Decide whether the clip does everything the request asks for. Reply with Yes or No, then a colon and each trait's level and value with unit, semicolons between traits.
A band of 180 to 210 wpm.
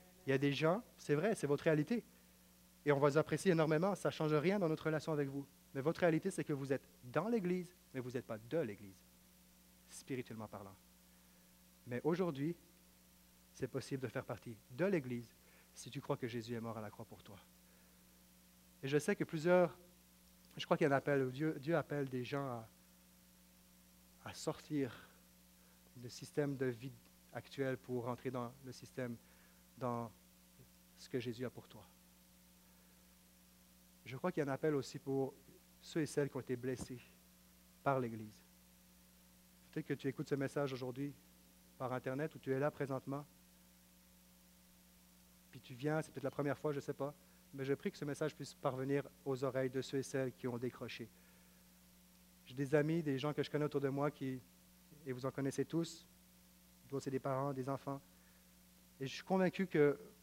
Yes: average, 185 wpm